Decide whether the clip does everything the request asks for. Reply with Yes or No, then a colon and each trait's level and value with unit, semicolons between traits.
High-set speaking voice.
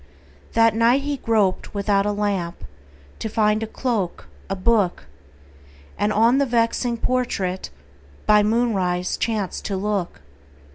Yes: high, 210 Hz